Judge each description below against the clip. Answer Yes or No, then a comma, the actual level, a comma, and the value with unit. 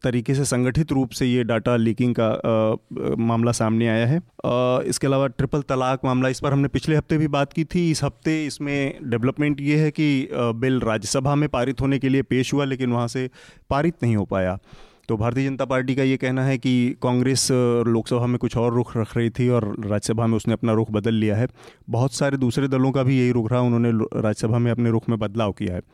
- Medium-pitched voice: No, low, 125 Hz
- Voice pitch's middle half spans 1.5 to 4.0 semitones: Yes, average, 2.9 semitones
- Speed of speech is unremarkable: No, fast, 230 wpm